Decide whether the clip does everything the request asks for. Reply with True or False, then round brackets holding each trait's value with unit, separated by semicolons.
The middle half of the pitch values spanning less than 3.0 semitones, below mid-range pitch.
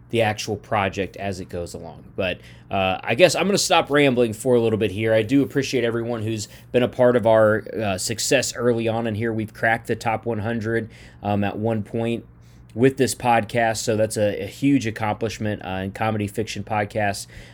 True (2.4 semitones; 110 Hz)